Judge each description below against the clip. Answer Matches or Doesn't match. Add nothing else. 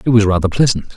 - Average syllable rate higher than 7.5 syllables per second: Matches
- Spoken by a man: Matches